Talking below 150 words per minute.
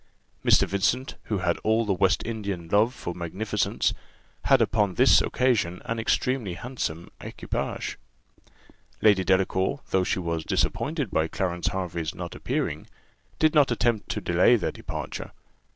Yes: average, 140 wpm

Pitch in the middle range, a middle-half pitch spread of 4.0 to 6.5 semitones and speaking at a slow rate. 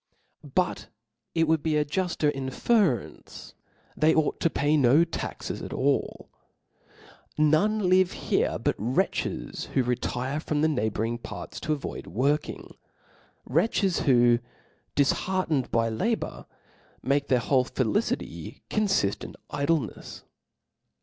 Yes: medium, 145 Hz; average, 4.8 semitones; slow, 130 wpm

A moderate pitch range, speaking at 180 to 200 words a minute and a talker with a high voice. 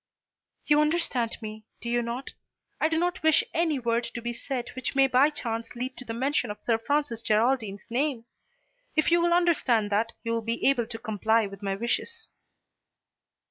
Yes: average, 4.2 semitones; average, 185 wpm; high, 240 Hz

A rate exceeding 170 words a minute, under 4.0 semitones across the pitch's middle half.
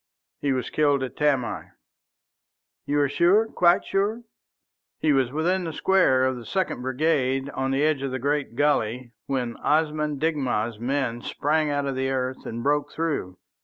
No: average, 165 wpm; average, 3.0 semitones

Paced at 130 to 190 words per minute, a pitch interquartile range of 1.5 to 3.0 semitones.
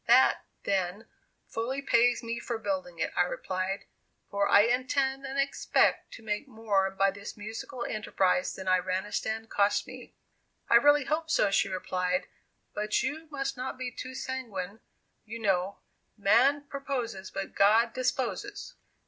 No: average, 145 wpm; average, 5.0 semitones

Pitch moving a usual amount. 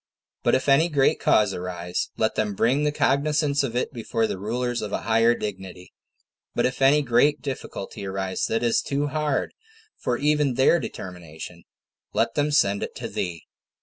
No: wide, 6.4 semitones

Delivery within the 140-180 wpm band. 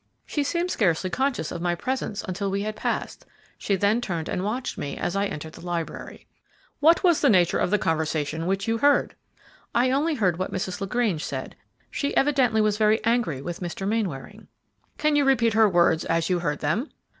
No: average, 195 wpm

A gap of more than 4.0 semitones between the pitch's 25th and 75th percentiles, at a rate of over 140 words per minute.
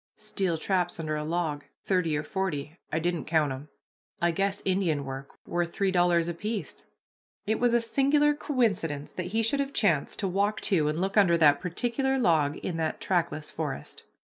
Yes: average, 4.7 semitones; average, 180 wpm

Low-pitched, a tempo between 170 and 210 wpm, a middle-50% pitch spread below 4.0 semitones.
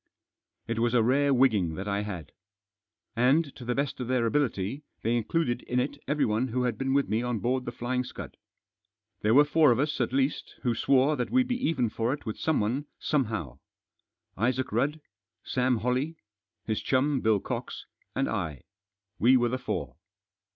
Yes: low, 125 Hz; average, 180 wpm; average, 3.4 semitones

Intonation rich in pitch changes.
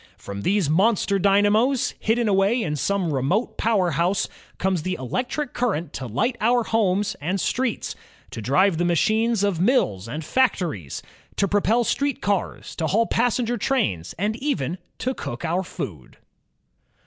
Yes: wide, 6.0 semitones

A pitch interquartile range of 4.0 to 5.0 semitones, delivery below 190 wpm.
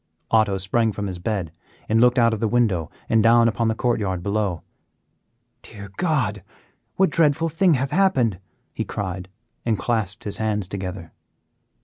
No: average, 3.6 semitones; average, 160 wpm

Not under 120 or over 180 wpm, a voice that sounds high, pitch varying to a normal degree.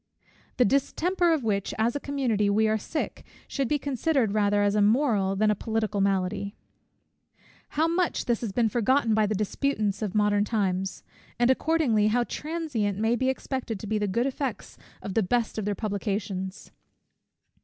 Yes: average, 175 wpm; high, 220 Hz; average, 4.3 semitones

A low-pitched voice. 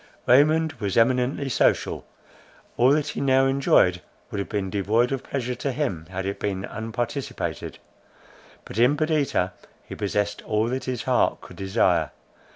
Yes: low, 120 Hz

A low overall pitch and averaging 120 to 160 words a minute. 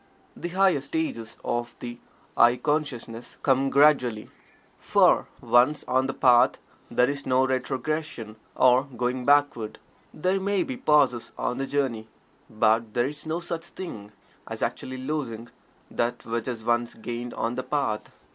Yes: low, 130 Hz; average, 145 wpm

